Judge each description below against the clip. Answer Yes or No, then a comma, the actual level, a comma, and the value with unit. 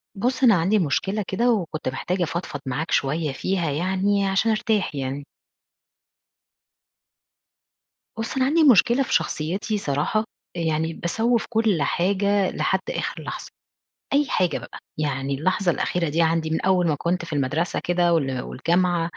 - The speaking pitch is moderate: Yes, medium, 175 Hz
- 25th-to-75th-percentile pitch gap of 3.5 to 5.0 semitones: Yes, average, 4.7 semitones